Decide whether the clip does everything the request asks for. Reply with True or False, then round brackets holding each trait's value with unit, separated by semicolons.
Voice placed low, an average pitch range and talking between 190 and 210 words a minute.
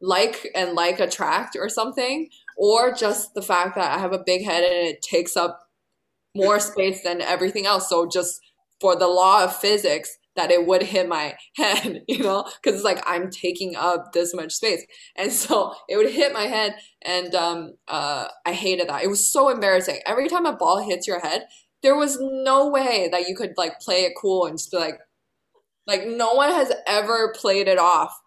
False (190 Hz; 4.4 semitones; 205 wpm)